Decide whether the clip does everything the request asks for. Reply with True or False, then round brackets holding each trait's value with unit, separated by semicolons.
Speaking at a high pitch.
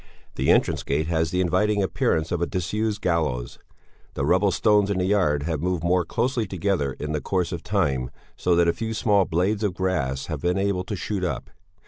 False (90 Hz)